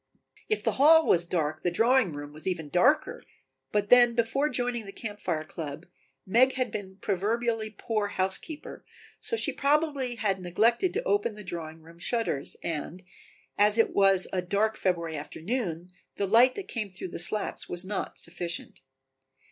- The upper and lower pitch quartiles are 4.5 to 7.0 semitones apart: Yes, wide, 5.6 semitones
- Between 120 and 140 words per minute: No, average, 170 wpm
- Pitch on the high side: Yes, high, 205 Hz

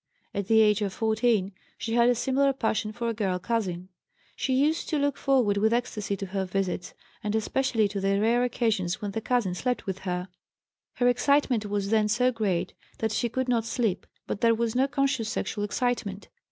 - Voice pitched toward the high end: Yes, high, 220 Hz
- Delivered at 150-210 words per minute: Yes, average, 195 wpm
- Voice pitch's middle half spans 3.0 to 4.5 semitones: Yes, average, 3.5 semitones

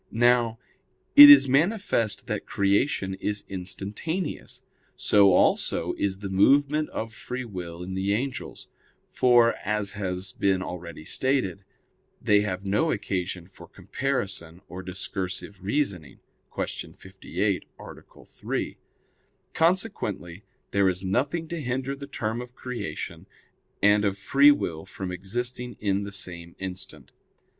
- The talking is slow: Yes, slow, 125 wpm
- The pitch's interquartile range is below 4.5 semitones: No, average, 5.2 semitones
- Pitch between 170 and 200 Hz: No, low, 100 Hz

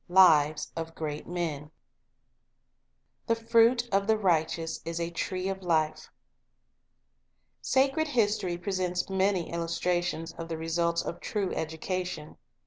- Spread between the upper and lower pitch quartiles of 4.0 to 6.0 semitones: No, average, 3.0 semitones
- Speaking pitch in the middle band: Yes, medium, 175 Hz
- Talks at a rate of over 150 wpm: No, average, 145 wpm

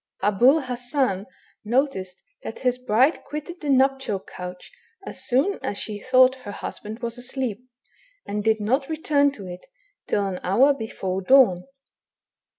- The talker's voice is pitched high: Yes, high, 245 Hz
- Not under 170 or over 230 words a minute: No, average, 145 wpm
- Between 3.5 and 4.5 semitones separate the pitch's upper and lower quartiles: No, average, 4.9 semitones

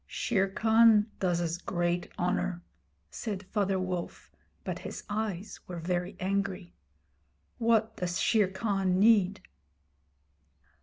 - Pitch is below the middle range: No, high, 190 Hz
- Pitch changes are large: No, average, 2.9 semitones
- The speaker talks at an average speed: No, slow, 110 wpm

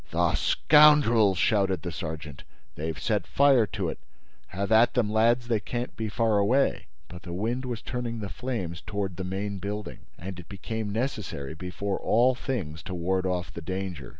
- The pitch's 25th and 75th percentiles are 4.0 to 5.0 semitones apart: Yes, average, 4.5 semitones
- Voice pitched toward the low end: Yes, low, 100 Hz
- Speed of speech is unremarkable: Yes, average, 180 wpm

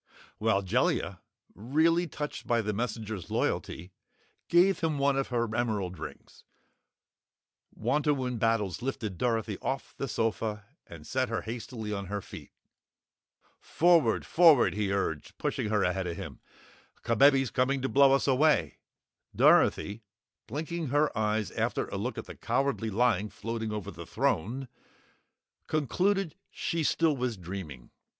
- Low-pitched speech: Yes, low, 115 Hz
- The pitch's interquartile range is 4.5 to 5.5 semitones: Yes, average, 5.1 semitones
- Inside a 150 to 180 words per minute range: No, slow, 135 wpm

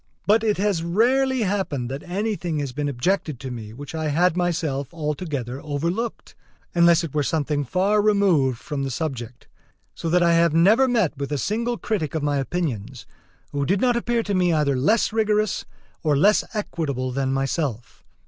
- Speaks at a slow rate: No, average, 175 wpm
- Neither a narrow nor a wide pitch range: No, wide, 6.4 semitones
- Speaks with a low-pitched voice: No, medium, 165 Hz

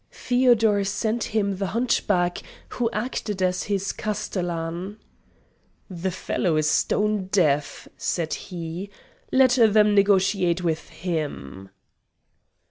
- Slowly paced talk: Yes, slow, 105 wpm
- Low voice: No, high, 195 Hz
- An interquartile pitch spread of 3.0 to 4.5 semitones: Yes, average, 3.6 semitones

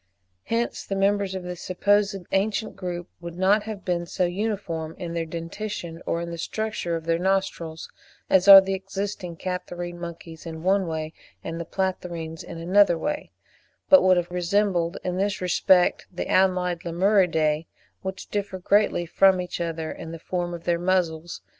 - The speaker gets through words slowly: No, average, 170 wpm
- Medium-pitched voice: Yes, medium, 180 Hz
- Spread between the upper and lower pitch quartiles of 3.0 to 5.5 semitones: No, narrow, 2.4 semitones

